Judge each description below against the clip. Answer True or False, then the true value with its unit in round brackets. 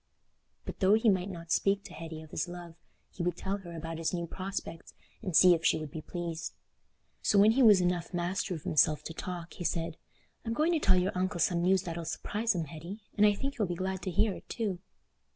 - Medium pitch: True (180 Hz)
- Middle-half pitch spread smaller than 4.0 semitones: True (3.0 semitones)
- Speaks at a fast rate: True (235 wpm)